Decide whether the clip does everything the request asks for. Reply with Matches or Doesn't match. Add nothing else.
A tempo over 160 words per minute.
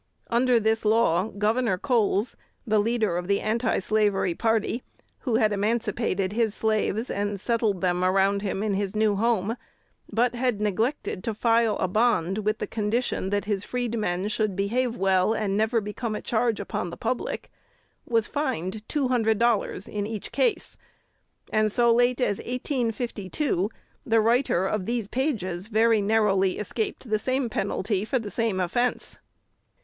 Doesn't match